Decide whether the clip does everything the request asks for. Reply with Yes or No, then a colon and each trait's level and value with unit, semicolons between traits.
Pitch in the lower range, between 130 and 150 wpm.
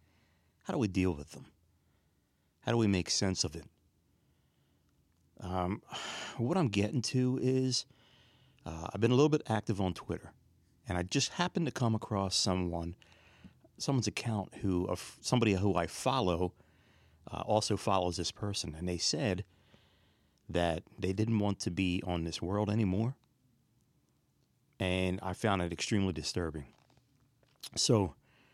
Yes: very low, 95 Hz; average, 145 wpm